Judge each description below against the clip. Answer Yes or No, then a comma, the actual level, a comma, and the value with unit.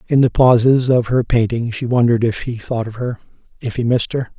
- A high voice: No, low, 120 Hz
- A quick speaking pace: Yes, fast, 230 wpm